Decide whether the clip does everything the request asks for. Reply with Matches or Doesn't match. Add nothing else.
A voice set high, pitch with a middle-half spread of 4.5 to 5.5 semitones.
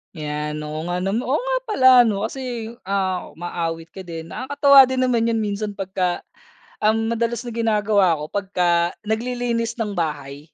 Matches